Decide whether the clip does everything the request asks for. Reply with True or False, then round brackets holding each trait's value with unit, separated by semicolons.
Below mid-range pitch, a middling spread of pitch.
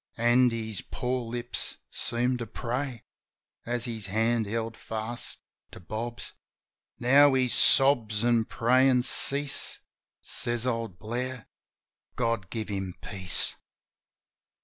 False (120 Hz; 2.2 semitones)